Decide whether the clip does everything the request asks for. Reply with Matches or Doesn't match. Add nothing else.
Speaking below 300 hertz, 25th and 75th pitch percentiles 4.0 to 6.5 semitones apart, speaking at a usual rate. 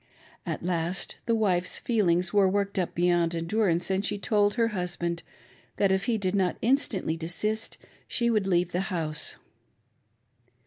Doesn't match